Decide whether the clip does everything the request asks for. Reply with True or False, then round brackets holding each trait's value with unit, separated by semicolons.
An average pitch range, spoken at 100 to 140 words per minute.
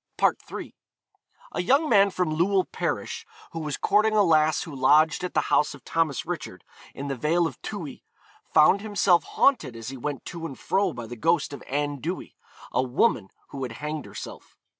False (4.6 semitones; 185 wpm)